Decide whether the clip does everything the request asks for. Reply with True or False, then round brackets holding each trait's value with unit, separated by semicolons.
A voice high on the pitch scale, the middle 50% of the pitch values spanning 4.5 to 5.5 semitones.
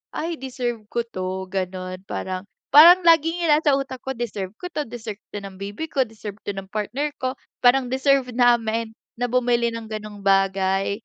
True (230 Hz; 5.1 semitones)